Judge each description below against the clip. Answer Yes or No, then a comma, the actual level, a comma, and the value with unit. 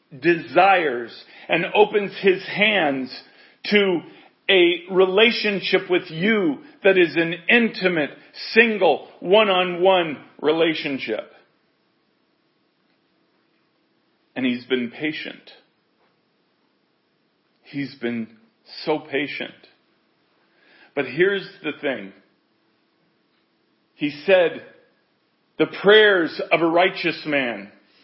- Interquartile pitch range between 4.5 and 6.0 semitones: Yes, average, 5.2 semitones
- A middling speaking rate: No, slow, 80 wpm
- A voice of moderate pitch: Yes, medium, 175 Hz